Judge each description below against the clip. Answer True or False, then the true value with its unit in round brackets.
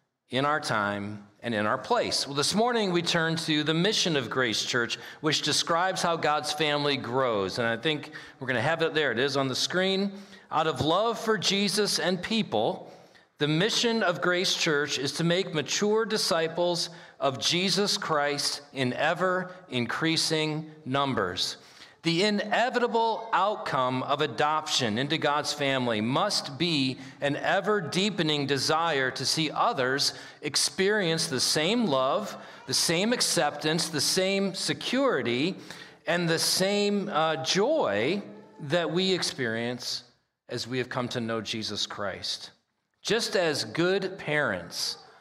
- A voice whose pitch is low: False (155 Hz)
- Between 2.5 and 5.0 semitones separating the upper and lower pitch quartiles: False (5.5 semitones)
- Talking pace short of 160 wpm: True (145 wpm)